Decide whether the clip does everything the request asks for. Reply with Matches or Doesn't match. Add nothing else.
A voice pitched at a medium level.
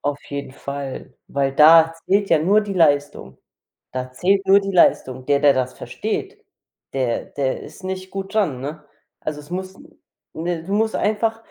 Matches